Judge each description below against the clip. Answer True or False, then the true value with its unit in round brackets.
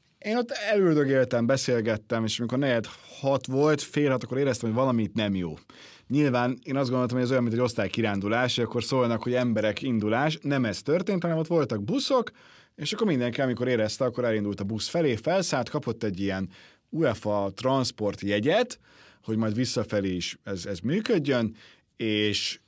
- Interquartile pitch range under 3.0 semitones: False (4.4 semitones)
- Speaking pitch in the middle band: False (120 Hz)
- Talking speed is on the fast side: True (170 wpm)